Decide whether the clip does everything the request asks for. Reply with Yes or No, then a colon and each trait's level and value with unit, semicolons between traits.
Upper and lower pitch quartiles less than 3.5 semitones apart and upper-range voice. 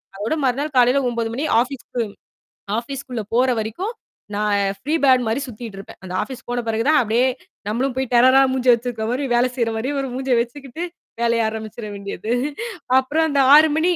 Yes: average, 3.1 semitones; high, 245 Hz